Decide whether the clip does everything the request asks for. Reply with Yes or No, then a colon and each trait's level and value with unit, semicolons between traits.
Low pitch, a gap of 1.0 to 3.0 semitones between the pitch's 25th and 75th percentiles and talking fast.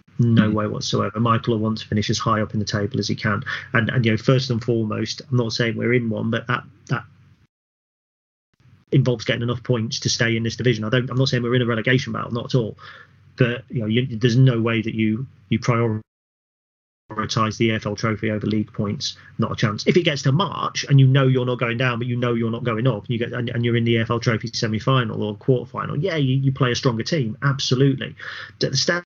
Yes: low, 120 Hz; narrow, 2.4 semitones; fast, 245 wpm